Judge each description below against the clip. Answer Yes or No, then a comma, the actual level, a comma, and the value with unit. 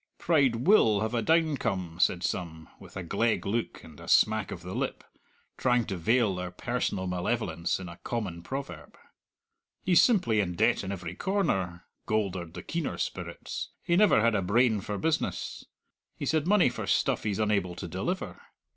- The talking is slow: No, average, 175 wpm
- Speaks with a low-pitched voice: Yes, low, 105 Hz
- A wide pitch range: Yes, wide, 5.7 semitones